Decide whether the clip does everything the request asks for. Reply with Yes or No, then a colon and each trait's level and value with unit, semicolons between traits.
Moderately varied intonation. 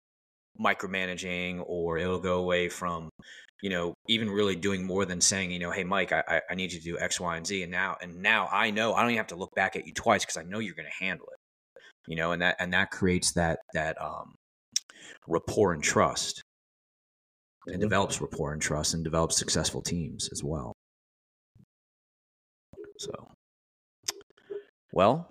No: narrow, 2.3 semitones